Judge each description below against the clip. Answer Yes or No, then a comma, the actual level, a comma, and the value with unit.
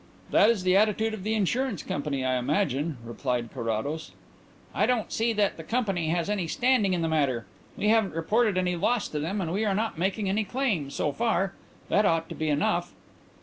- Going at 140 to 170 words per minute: No, average, 200 wpm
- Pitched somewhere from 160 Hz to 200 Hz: Yes, medium, 185 Hz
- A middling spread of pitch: No, wide, 5.7 semitones